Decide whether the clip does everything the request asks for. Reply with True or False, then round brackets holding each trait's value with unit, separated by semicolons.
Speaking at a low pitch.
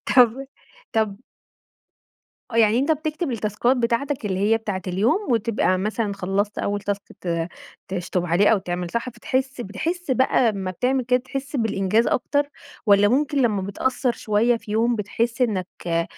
False (225 Hz)